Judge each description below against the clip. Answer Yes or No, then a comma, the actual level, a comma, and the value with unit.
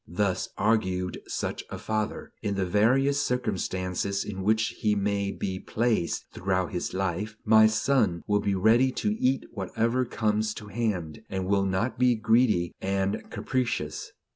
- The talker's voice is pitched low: Yes, low, 105 Hz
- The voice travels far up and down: No, average, 3.2 semitones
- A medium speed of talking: Yes, average, 150 wpm